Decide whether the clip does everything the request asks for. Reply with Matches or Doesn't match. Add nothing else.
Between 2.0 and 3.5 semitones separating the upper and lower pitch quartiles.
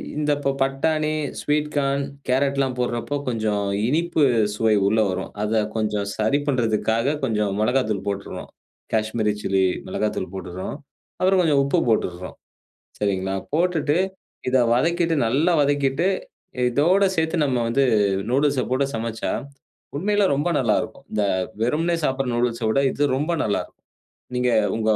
Doesn't match